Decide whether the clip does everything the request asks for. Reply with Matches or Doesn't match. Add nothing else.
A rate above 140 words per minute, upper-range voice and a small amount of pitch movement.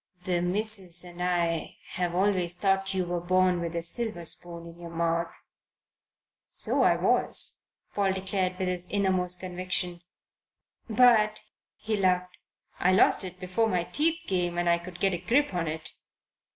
Doesn't match